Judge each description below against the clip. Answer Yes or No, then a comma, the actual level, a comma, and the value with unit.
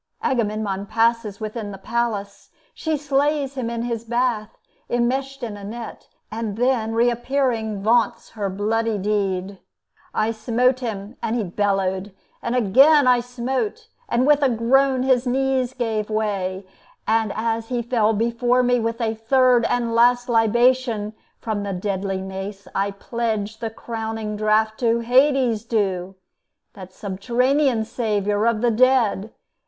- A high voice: Yes, high, 230 Hz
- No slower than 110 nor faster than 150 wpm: Yes, average, 140 wpm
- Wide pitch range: No, average, 2.9 semitones